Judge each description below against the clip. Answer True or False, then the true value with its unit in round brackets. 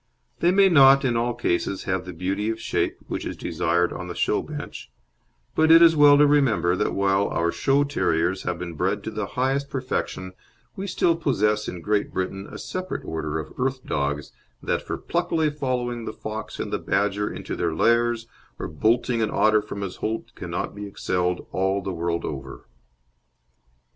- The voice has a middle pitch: False (105 Hz)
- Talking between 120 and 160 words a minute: False (185 wpm)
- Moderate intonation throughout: False (6.7 semitones)